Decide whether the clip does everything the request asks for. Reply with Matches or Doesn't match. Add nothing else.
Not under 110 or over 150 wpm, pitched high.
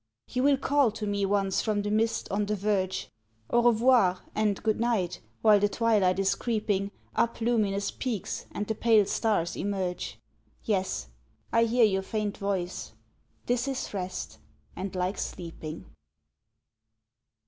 Matches